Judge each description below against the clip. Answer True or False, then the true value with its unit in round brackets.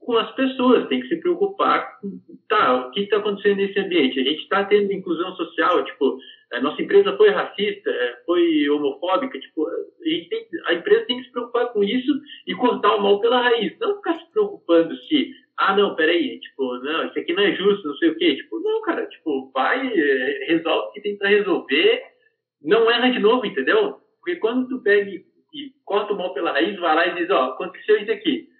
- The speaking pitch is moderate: False (260 Hz)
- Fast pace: True (205 wpm)